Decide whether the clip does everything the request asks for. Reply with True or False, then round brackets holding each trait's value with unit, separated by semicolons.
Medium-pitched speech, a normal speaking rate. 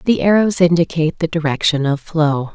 True (165 Hz; 165 wpm)